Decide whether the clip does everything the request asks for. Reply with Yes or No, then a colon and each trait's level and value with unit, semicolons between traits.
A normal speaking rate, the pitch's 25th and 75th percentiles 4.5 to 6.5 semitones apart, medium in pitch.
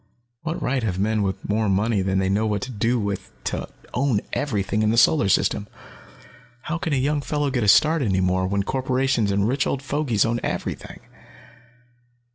No: average, 190 wpm; average, 5.1 semitones; low, 110 Hz